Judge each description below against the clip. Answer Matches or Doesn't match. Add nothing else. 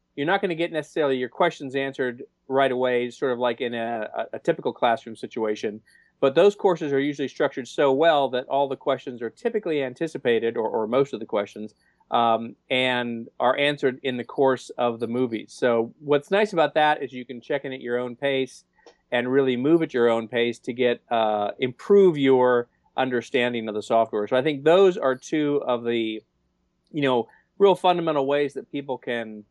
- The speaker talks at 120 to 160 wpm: Doesn't match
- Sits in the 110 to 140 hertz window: Matches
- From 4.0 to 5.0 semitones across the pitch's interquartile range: Doesn't match